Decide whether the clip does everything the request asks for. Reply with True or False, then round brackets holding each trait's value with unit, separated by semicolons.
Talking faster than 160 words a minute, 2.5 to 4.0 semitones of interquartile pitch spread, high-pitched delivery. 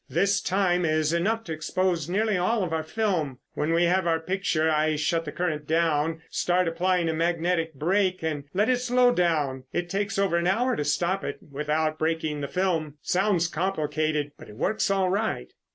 False (195 wpm; 3.4 semitones; 170 Hz)